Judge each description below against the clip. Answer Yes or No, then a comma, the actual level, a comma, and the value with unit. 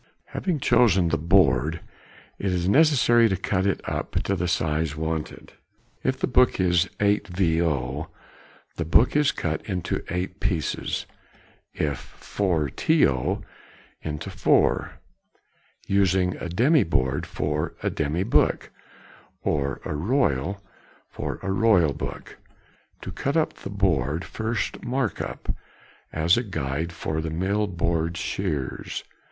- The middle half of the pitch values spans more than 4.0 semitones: Yes, average, 4.5 semitones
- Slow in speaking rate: Yes, slow, 130 wpm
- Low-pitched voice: Yes, very low, 90 Hz